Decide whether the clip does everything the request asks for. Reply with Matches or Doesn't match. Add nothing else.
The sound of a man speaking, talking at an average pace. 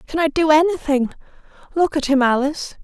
Doesn't match